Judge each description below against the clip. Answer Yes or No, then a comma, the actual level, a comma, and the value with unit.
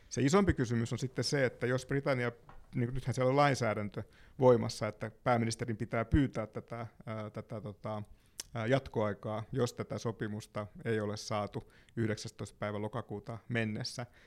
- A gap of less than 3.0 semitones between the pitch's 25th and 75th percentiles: Yes, narrow, 2.6 semitones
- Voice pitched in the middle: No, low, 115 Hz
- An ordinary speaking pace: Yes, average, 135 wpm